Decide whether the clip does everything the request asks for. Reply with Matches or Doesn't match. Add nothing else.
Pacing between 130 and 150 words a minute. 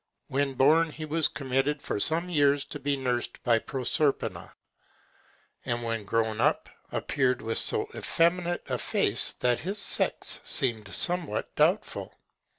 Matches